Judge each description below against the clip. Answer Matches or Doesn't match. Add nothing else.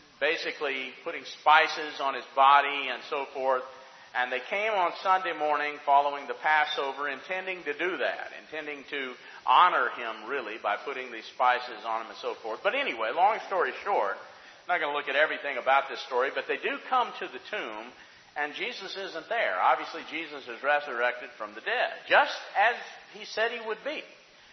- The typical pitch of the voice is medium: Matches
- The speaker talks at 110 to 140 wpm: Doesn't match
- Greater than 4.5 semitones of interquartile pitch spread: Matches